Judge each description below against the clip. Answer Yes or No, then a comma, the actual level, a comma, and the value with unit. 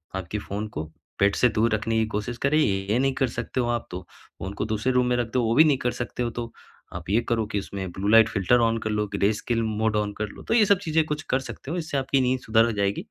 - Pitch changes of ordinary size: Yes, average, 3.5 semitones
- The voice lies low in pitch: Yes, low, 115 Hz